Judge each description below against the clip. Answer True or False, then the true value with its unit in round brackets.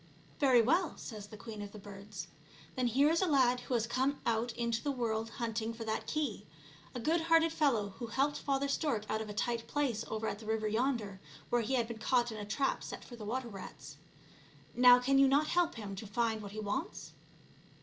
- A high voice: True (235 Hz)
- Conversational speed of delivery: False (230 wpm)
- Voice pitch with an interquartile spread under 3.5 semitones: False (4.0 semitones)